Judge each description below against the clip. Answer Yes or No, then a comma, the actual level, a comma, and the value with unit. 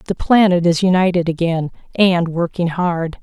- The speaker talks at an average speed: Yes, average, 150 wpm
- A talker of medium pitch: Yes, medium, 175 Hz